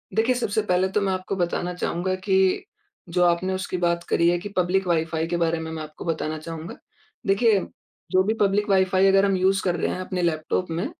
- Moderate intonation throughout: No, narrow, 2.2 semitones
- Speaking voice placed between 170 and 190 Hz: Yes, medium, 185 Hz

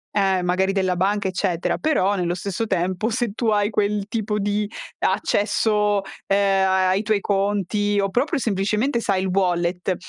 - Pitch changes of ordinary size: No, narrow, 1.9 semitones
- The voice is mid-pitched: No, high, 200 Hz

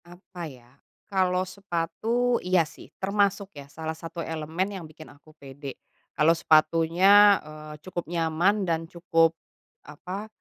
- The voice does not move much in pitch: No, average, 3.3 semitones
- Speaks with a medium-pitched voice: Yes, medium, 170 Hz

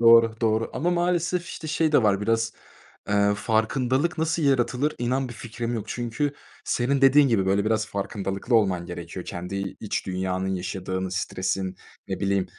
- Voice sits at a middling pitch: No, low, 110 Hz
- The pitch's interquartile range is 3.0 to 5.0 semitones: No, wide, 5.5 semitones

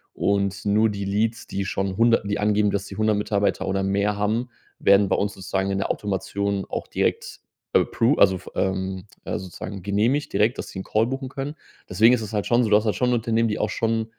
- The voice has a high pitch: No, low, 105 Hz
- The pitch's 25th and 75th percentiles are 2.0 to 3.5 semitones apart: Yes, narrow, 2.4 semitones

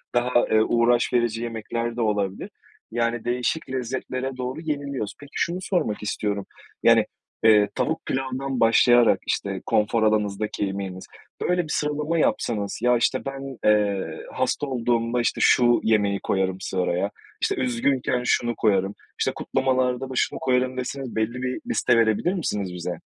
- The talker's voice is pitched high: No, low, 120 Hz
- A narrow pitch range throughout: No, average, 3.6 semitones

